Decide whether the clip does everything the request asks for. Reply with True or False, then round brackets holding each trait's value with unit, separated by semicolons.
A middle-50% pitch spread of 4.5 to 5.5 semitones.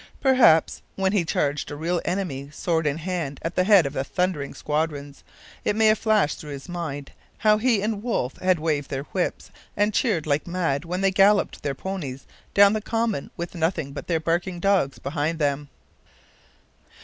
True (5.2 semitones)